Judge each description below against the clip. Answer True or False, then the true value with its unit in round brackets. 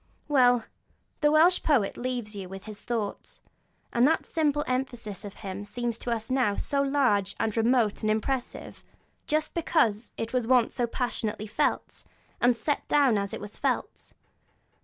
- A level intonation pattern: False (4.2 semitones)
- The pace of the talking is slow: False (160 wpm)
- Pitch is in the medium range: False (240 Hz)